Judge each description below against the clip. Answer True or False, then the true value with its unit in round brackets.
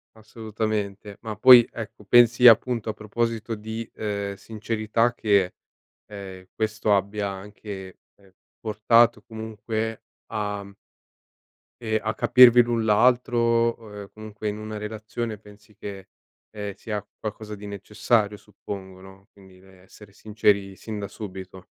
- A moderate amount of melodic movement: False (1.7 semitones)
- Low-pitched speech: True (105 Hz)